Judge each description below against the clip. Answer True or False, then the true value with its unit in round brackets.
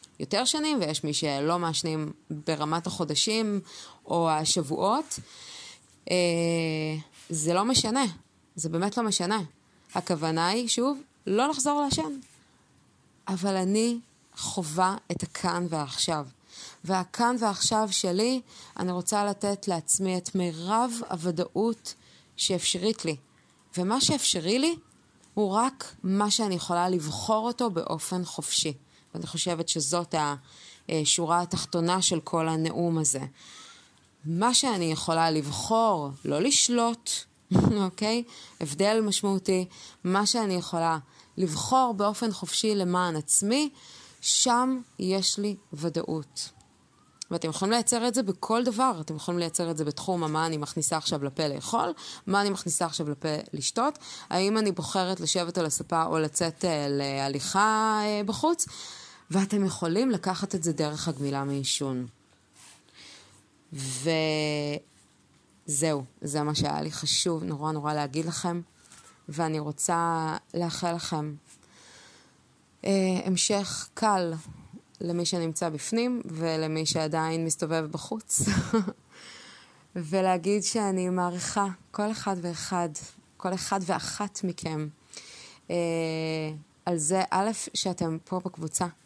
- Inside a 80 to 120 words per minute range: True (115 wpm)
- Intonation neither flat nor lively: True (4.3 semitones)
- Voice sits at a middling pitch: True (175 Hz)